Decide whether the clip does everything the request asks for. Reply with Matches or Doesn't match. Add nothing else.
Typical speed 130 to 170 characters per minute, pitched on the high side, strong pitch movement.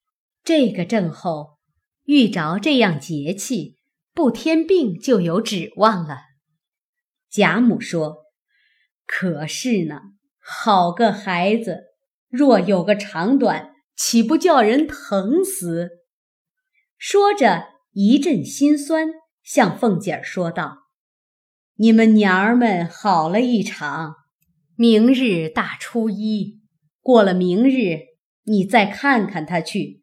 Matches